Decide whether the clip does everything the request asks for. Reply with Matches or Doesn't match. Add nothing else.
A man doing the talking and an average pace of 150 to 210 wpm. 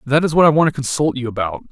Doesn't match